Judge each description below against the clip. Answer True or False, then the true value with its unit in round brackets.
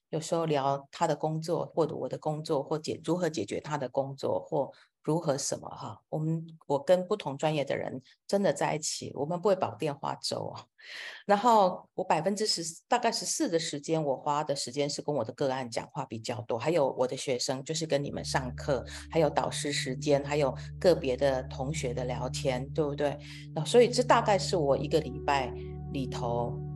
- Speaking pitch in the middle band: True (145 Hz)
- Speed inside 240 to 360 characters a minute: True (290 characters per minute)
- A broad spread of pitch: False (3.2 semitones)